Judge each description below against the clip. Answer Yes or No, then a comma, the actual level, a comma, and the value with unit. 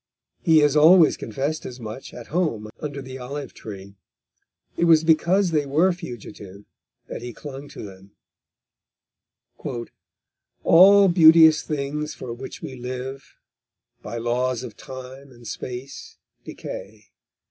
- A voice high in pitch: No, low, 135 Hz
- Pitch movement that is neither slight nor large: Yes, average, 4.5 semitones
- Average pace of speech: No, slow, 125 wpm